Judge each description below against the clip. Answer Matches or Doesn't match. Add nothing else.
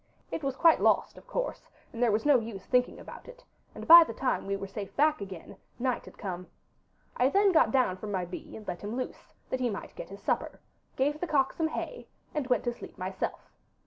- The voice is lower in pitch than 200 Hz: Doesn't match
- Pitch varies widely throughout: Matches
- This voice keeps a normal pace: Doesn't match